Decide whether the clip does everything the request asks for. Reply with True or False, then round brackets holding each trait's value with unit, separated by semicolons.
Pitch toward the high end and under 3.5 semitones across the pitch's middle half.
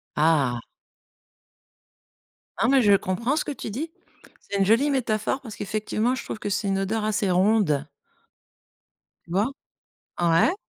False (210 Hz; 3.9 semitones)